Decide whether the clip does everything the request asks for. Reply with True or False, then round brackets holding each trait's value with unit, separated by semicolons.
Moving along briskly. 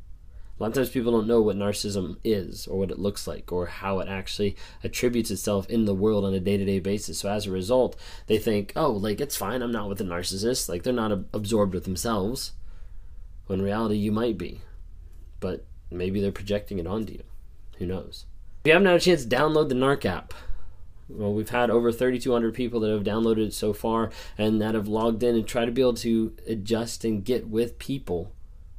True (215 wpm)